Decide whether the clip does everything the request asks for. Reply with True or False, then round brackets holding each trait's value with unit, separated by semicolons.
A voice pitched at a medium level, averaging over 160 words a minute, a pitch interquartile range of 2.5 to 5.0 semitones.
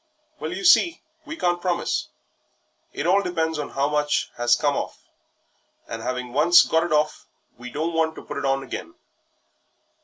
True (160 Hz; 175 wpm; 4.3 semitones)